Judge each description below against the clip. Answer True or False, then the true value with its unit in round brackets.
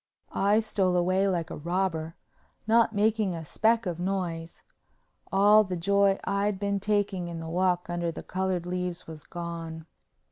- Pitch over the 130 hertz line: True (185 Hz)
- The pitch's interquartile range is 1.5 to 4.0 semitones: True (2.8 semitones)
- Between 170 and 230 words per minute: False (155 wpm)